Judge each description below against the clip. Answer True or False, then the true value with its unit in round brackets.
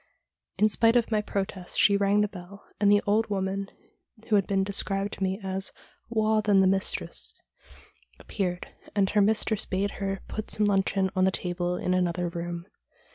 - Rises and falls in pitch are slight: True (1.7 semitones)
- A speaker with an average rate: True (185 wpm)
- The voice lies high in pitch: True (195 Hz)